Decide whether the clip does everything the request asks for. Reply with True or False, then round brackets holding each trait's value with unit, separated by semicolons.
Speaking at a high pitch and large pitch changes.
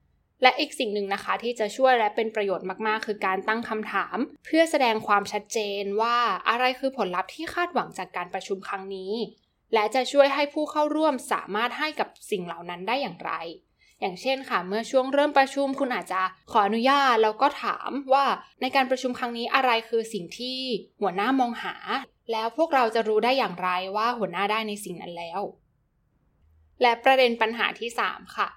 False (230 Hz; 4.6 semitones)